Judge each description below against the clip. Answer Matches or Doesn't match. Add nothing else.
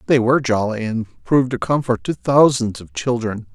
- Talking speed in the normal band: Matches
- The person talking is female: Doesn't match